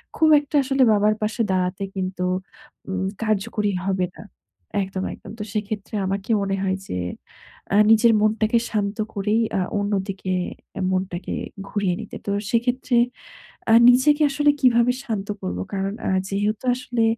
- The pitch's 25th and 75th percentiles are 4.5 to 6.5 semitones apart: No, average, 3.2 semitones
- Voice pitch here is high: Yes, high, 210 Hz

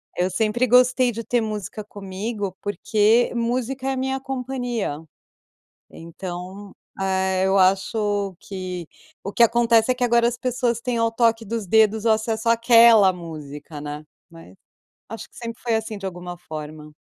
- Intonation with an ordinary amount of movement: Yes, average, 4.0 semitones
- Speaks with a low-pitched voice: No, high, 220 Hz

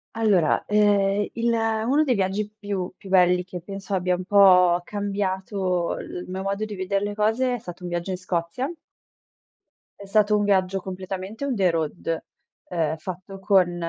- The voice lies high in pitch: Yes, high, 195 Hz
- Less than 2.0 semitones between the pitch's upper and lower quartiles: No, narrow, 2.4 semitones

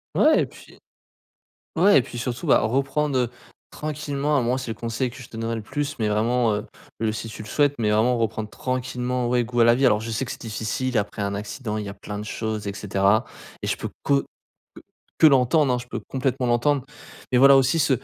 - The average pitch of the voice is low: Yes, low, 120 Hz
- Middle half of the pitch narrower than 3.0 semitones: No, average, 3.3 semitones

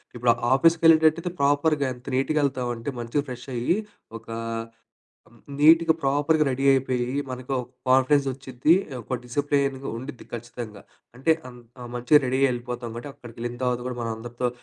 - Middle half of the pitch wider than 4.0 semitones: No, average, 2.9 semitones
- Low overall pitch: Yes, low, 130 Hz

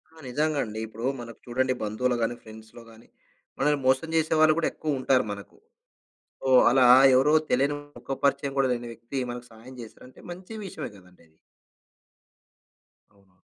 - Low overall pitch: Yes, low, 125 Hz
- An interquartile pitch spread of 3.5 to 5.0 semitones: Yes, average, 3.9 semitones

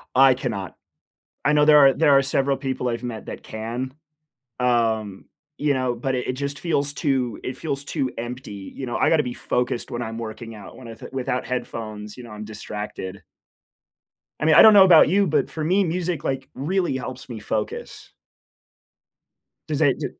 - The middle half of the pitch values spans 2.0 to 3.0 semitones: No, average, 3.9 semitones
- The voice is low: Yes, low, 130 Hz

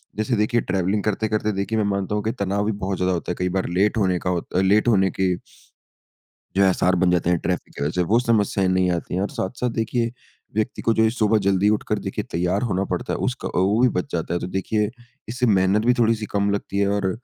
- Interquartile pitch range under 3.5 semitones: Yes, average, 2.8 semitones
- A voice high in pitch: No, low, 100 Hz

